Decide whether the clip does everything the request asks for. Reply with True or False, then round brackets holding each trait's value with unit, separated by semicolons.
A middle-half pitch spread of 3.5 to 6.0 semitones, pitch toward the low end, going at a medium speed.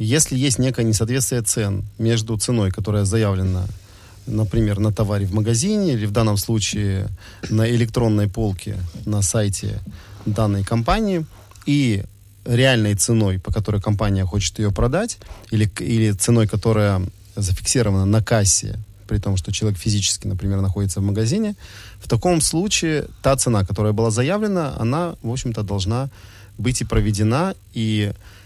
False (2.7 semitones; 110 Hz; 140 wpm)